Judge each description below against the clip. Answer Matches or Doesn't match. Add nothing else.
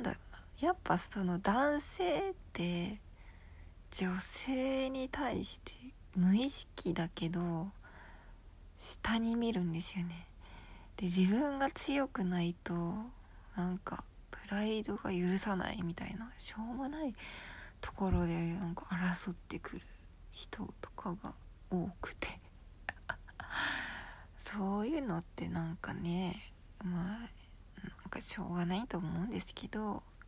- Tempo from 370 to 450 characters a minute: Doesn't match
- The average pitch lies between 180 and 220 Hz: Matches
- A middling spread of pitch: Matches